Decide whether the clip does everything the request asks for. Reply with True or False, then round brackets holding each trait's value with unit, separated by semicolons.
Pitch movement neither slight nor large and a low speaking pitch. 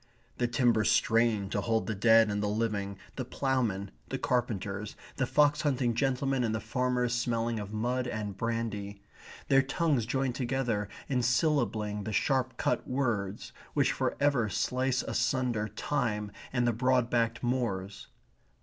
True (3.1 semitones; 120 Hz)